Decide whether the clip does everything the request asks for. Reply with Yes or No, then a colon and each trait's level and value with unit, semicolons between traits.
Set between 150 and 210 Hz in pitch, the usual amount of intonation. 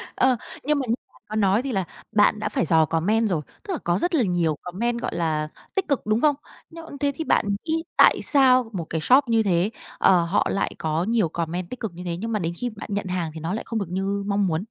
No: high, 205 Hz; wide, 6.0 semitones